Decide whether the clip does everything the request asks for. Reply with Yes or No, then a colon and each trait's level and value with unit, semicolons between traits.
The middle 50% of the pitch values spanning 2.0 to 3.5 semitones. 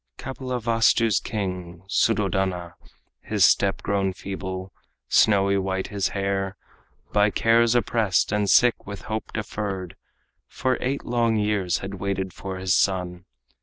Yes: average, 2.7 semitones